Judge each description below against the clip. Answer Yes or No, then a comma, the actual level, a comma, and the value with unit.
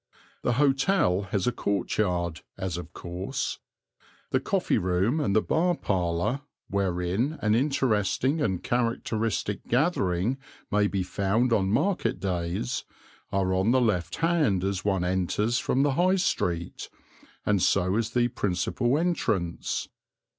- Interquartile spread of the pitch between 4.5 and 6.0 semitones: Yes, wide, 5.6 semitones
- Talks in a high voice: No, low, 105 Hz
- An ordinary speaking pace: No, slow, 130 wpm